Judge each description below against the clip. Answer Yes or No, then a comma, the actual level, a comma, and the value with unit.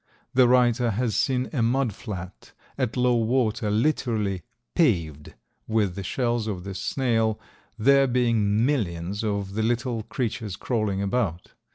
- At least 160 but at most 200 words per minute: No, average, 140 wpm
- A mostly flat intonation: No, average, 3.6 semitones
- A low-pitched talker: Yes, low, 115 Hz